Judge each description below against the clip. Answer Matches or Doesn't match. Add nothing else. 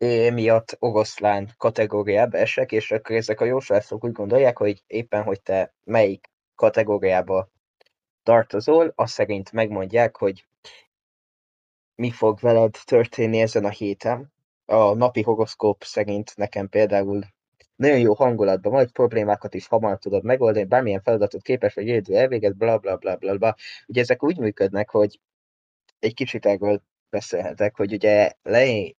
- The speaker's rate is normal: Matches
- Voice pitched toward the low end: Matches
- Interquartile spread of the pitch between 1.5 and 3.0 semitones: Matches